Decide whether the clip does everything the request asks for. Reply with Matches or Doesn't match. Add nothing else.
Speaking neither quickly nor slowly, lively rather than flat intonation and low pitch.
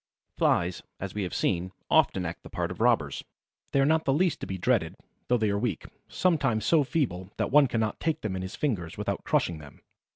Doesn't match